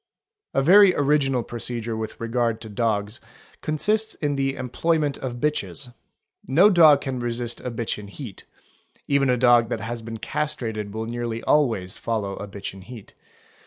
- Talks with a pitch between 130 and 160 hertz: No, low, 120 Hz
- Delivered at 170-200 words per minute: Yes, average, 175 wpm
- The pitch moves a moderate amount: Yes, average, 3.9 semitones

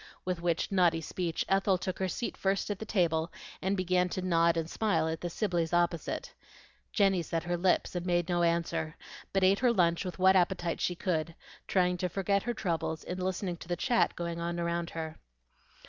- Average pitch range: No, narrow, 1.9 semitones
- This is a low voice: No, medium, 175 Hz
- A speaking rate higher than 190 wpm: Yes, average, 200 wpm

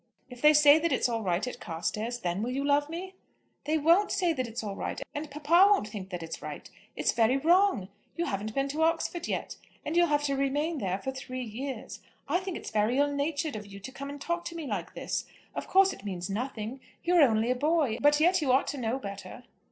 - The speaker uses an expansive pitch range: Yes, wide, 6.2 semitones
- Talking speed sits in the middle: No, fast, 240 wpm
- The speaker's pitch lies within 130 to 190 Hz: No, very high, 275 Hz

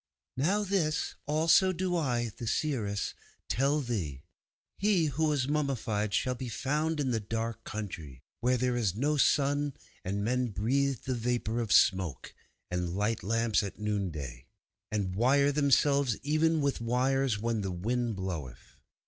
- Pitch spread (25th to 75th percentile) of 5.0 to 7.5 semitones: Yes, wide, 5.5 semitones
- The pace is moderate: Yes, average, 150 wpm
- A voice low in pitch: Yes, low, 120 Hz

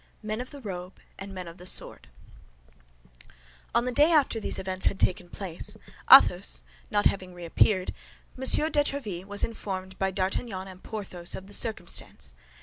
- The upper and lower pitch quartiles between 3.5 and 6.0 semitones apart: No, average, 3.1 semitones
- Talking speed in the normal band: Yes, average, 160 wpm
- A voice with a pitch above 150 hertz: Yes, high, 190 Hz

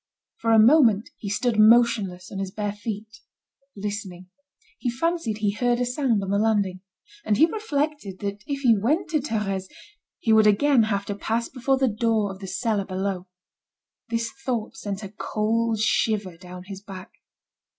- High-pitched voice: Yes, high, 215 Hz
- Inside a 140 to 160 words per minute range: No, average, 170 wpm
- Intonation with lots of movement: No, average, 3.2 semitones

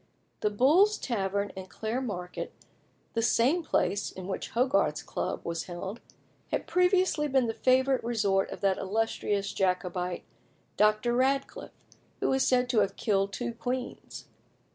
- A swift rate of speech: No, average, 145 wpm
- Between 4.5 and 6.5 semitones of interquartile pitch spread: Yes, average, 4.8 semitones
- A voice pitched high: Yes, high, 225 Hz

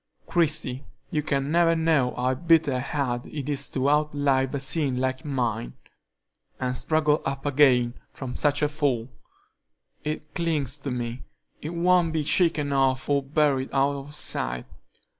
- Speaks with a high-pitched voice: No, medium, 140 Hz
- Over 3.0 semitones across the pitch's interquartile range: No, average, 2.7 semitones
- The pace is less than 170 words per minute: Yes, average, 150 wpm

